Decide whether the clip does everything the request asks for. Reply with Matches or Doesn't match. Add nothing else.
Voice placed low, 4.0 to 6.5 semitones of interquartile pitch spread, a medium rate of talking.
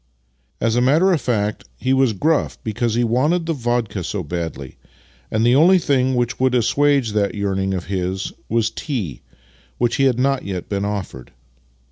Matches